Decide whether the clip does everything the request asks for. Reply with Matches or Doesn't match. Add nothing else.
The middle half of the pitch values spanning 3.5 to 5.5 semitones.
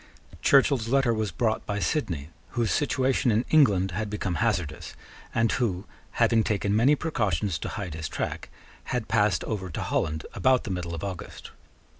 Matches